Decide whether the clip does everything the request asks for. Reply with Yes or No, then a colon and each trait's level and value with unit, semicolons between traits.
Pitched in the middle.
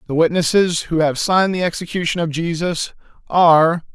Yes: medium, 165 Hz